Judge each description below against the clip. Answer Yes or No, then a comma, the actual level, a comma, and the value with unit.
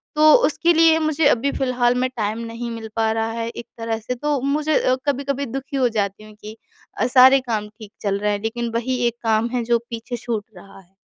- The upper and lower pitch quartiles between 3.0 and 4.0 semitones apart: Yes, average, 3.4 semitones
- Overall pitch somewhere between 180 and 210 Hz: No, high, 235 Hz